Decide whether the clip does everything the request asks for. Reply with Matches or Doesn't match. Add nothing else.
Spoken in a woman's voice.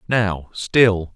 Doesn't match